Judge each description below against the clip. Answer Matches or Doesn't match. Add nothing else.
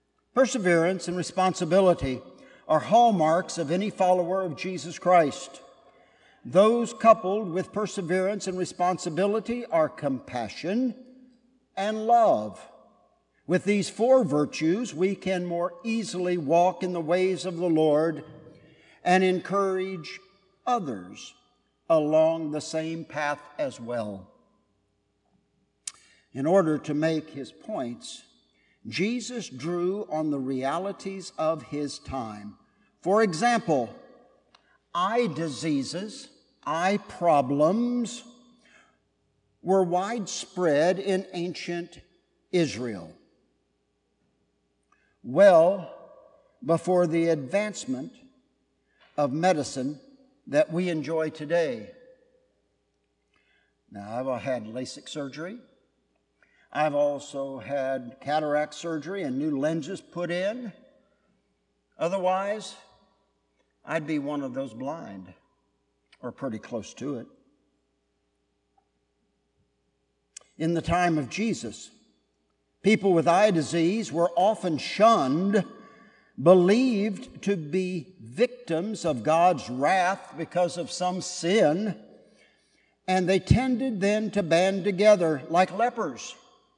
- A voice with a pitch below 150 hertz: Doesn't match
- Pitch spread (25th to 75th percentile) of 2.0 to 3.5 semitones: Doesn't match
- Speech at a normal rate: Doesn't match